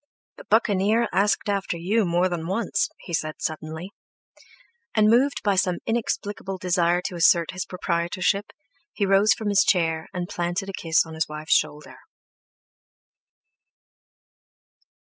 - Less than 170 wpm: Yes, slow, 135 wpm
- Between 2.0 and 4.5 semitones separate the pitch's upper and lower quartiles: Yes, average, 3.2 semitones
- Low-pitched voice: No, medium, 185 Hz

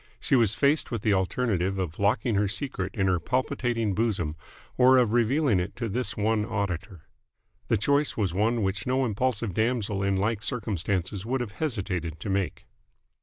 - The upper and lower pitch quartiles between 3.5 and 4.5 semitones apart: Yes, average, 4.0 semitones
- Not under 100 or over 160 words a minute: No, average, 170 wpm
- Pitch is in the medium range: No, low, 105 Hz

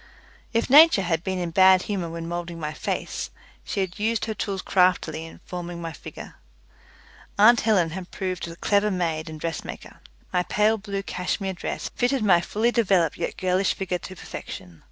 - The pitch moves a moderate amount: Yes, average, 3.4 semitones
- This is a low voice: No, medium, 185 Hz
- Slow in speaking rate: No, average, 175 wpm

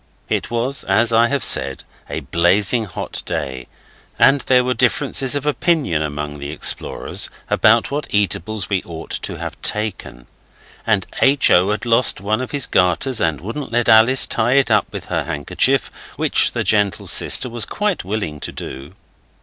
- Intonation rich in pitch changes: Yes, wide, 6.4 semitones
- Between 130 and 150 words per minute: No, average, 170 wpm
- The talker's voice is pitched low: Yes, low, 110 Hz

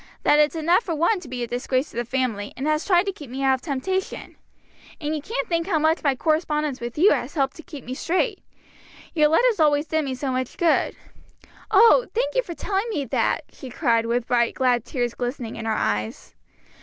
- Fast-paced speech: Yes, fast, 220 wpm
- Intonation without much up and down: No, average, 5.2 semitones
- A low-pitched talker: No, very high, 295 Hz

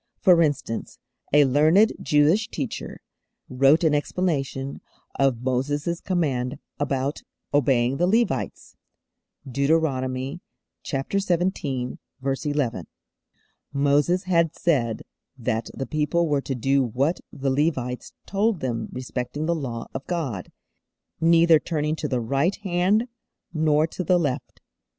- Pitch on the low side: No, medium, 145 Hz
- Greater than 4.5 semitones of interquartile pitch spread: No, average, 4.2 semitones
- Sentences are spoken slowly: Yes, slow, 115 wpm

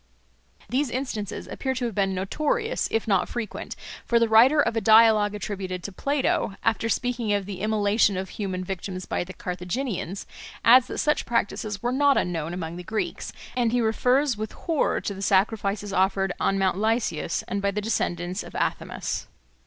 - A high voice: Yes, high, 210 Hz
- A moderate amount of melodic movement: Yes, average, 3.7 semitones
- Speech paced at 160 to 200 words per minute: Yes, average, 175 wpm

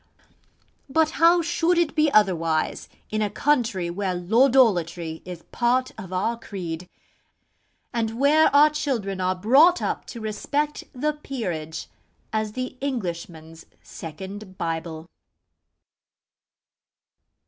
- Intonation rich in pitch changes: Yes, wide, 7.9 semitones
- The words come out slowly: Yes, slow, 110 wpm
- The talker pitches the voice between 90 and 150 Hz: No, high, 215 Hz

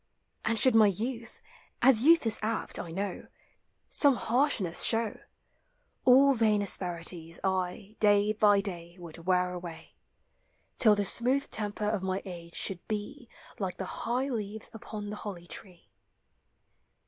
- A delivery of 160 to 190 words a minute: No, average, 150 wpm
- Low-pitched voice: No, high, 205 Hz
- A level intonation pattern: No, average, 3.9 semitones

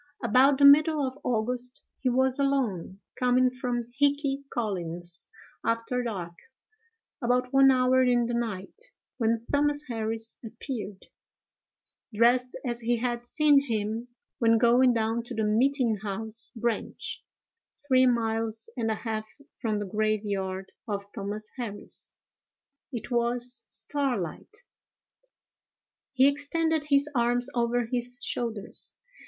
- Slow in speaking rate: Yes, slow, 120 wpm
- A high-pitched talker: Yes, high, 240 Hz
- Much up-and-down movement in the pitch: No, average, 2.9 semitones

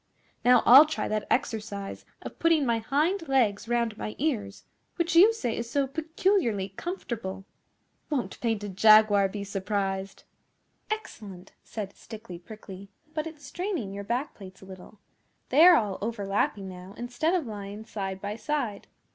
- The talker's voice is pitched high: Yes, high, 220 Hz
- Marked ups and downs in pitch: Yes, wide, 6.2 semitones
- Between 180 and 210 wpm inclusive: No, average, 150 wpm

